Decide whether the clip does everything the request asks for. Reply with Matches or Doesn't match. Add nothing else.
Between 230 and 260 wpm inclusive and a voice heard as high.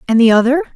Matches